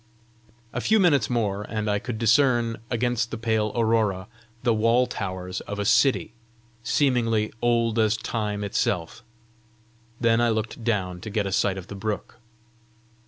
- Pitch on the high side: No, low, 110 Hz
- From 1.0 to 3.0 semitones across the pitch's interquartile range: Yes, narrow, 2.4 semitones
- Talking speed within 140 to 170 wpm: Yes, average, 155 wpm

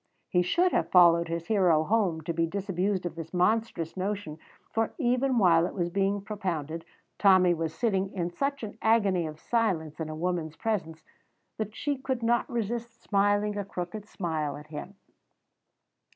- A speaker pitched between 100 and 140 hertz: No, high, 190 Hz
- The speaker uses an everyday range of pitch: Yes, average, 4.6 semitones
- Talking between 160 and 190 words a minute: Yes, average, 165 wpm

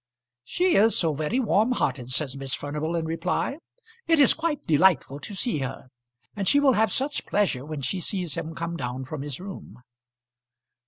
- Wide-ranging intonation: Yes, wide, 7.4 semitones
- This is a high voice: No, medium, 165 Hz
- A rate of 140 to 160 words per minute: No, average, 180 wpm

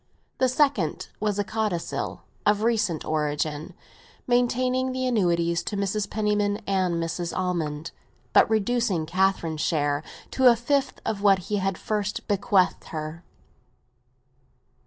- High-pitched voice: Yes, high, 200 Hz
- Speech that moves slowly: Yes, slow, 125 wpm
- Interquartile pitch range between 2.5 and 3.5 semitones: No, average, 4.6 semitones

